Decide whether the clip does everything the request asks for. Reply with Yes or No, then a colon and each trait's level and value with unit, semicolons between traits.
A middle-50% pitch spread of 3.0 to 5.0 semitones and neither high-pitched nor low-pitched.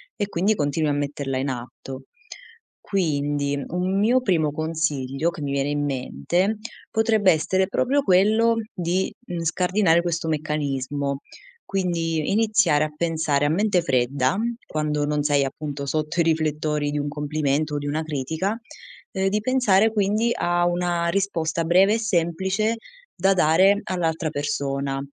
Yes: average, 4.6 semitones; medium, 160 Hz